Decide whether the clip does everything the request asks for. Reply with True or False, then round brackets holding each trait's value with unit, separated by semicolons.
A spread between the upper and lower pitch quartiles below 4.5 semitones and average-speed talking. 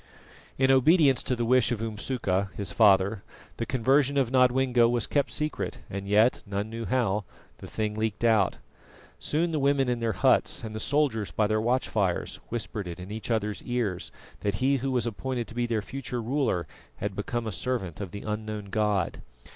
True (3.6 semitones; 190 wpm)